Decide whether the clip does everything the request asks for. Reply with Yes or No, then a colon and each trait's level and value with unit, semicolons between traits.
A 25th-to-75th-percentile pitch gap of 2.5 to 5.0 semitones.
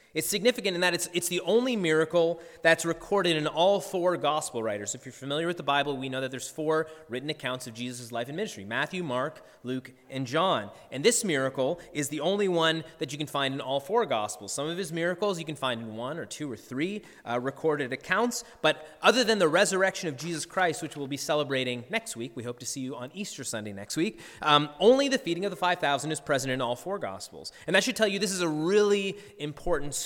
No: wide, 5.6 semitones